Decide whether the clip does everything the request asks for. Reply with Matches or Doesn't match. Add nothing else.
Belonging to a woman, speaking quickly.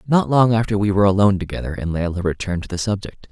Doesn't match